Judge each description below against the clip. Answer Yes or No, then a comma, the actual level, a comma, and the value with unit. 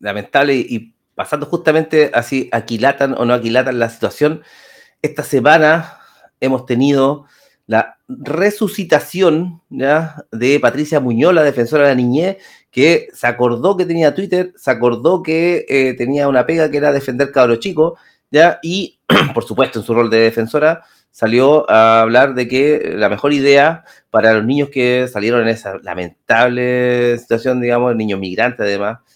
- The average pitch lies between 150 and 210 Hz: No, low, 135 Hz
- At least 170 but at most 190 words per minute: No, average, 155 wpm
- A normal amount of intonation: Yes, average, 4.3 semitones